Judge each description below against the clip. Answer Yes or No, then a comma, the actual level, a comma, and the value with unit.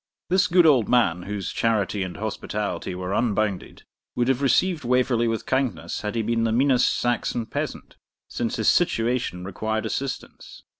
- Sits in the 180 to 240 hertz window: No, low, 115 Hz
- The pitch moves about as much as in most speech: Yes, average, 3.5 semitones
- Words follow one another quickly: No, average, 155 wpm